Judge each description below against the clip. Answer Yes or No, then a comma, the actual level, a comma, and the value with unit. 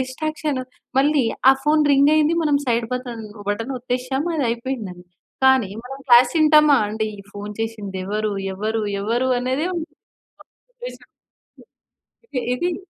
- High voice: Yes, very high, 255 Hz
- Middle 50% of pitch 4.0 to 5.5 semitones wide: Yes, average, 5.0 semitones